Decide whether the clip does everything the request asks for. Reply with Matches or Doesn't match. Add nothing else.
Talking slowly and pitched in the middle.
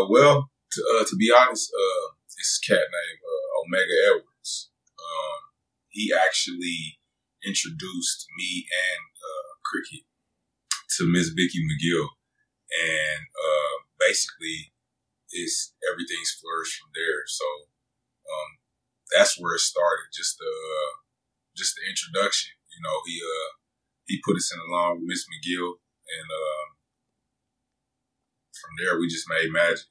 Matches